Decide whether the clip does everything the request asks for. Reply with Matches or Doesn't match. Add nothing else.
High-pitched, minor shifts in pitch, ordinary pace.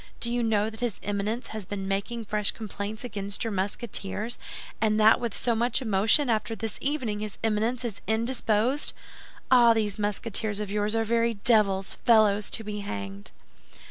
Matches